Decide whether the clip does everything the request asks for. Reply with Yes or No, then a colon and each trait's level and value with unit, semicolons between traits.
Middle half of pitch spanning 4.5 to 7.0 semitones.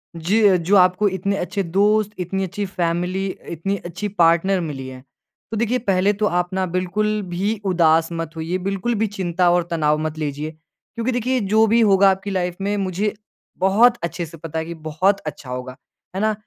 No: average, 3.5 semitones